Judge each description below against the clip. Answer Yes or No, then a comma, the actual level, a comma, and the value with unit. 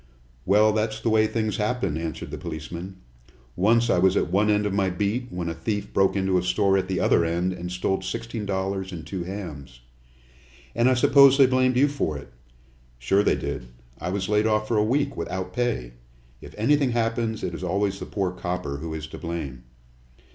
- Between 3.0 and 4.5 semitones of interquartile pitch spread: Yes, average, 3.9 semitones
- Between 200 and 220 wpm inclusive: Yes, fast, 205 wpm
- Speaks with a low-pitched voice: Yes, very low, 95 Hz